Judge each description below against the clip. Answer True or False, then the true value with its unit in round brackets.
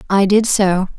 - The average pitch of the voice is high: True (195 Hz)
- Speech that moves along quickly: False (185 wpm)